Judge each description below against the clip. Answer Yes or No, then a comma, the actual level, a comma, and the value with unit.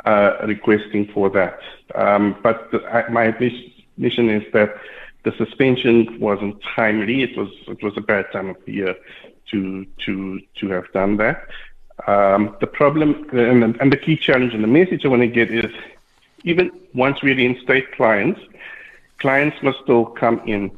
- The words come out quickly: No, average, 180 wpm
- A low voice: Yes, low, 115 Hz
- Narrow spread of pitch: No, average, 3.8 semitones